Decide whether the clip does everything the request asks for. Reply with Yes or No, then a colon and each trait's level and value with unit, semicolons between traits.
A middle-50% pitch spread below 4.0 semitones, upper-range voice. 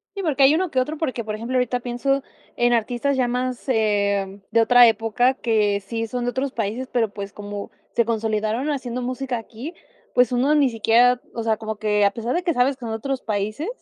Yes: average, 2.9 semitones; high, 240 Hz